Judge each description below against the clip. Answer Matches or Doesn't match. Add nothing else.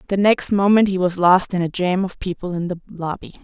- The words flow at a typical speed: Doesn't match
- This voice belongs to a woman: Matches